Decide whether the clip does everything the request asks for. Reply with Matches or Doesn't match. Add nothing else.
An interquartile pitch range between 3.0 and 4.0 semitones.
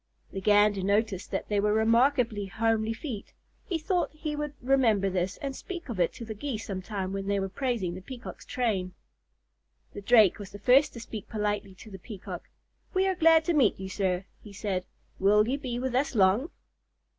Doesn't match